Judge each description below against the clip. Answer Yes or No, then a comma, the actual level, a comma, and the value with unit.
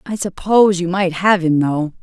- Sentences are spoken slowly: No, fast, 205 wpm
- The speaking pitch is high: No, medium, 180 Hz